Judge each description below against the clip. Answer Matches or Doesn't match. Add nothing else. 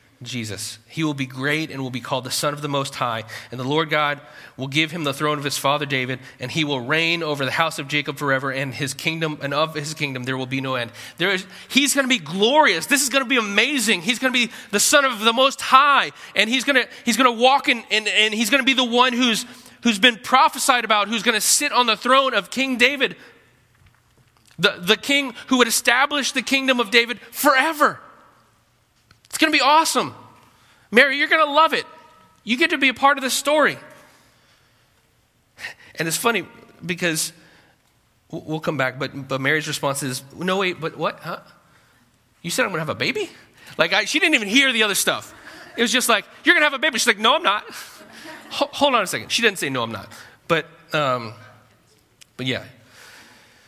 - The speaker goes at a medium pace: Doesn't match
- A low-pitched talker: Doesn't match